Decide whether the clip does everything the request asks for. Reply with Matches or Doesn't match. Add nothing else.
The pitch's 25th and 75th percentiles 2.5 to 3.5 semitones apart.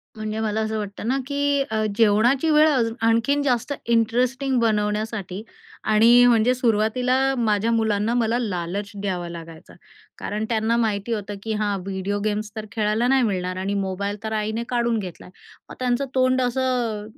Matches